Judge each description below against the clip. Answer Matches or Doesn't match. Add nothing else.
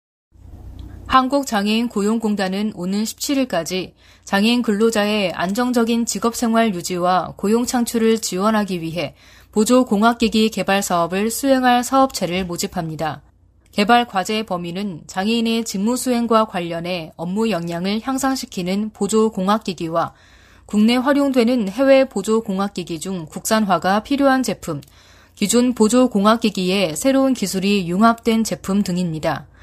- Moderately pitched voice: Doesn't match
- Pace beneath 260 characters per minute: Doesn't match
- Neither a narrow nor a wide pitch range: Matches